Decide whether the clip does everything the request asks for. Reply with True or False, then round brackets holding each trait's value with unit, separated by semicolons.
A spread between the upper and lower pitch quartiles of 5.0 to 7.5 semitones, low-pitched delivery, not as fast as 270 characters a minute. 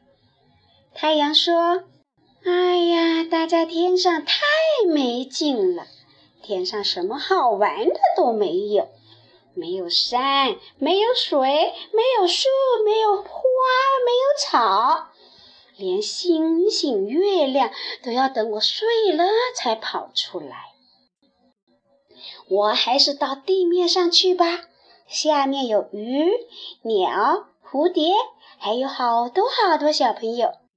False (5.6 semitones; 335 Hz; 150 characters per minute)